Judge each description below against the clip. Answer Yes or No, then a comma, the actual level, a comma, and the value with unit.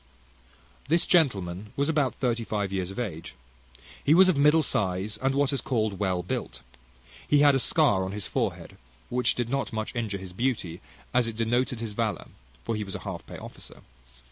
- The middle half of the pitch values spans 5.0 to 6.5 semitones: Yes, wide, 5.6 semitones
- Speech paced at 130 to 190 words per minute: No, average, 200 wpm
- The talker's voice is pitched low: Yes, low, 115 Hz